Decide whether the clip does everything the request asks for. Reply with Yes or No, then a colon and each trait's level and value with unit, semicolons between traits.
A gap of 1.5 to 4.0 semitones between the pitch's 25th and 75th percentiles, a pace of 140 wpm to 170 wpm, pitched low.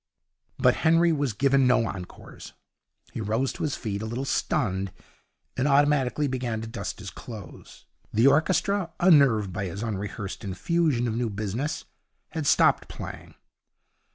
No: wide, 5.5 semitones; average, 145 wpm; low, 125 Hz